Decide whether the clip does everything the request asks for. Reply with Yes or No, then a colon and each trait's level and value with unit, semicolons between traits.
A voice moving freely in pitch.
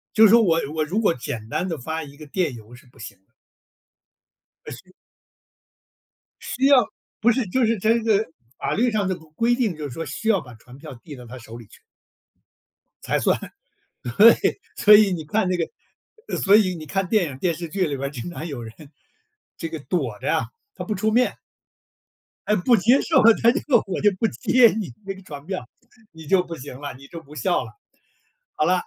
Yes: wide, 7.1 semitones